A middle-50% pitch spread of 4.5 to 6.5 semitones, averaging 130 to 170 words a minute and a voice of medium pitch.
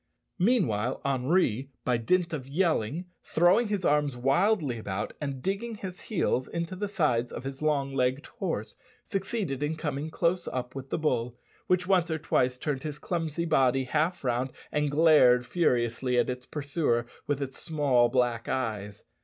Yes: average, 5.2 semitones; average, 160 wpm; medium, 145 Hz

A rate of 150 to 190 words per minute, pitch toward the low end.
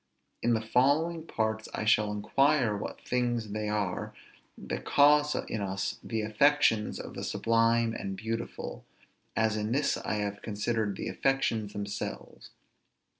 No: average, 140 wpm; low, 110 Hz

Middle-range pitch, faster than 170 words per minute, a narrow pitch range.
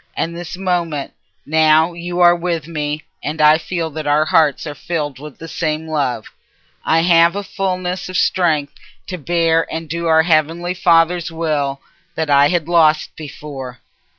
No: medium, 160 Hz; average, 165 wpm; narrow, 2.3 semitones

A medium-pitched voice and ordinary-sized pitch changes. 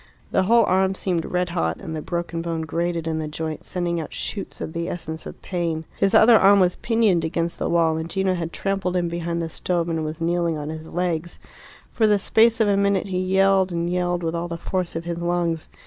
No: medium, 175 Hz; narrow, 2.3 semitones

